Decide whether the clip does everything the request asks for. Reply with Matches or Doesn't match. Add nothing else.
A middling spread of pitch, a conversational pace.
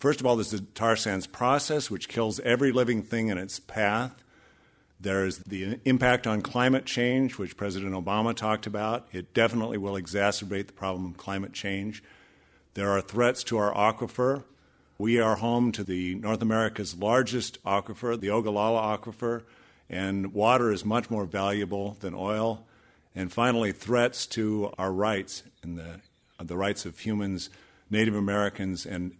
Matches